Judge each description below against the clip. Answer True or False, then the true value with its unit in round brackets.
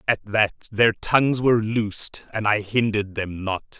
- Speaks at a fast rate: False (175 wpm)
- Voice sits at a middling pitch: False (105 Hz)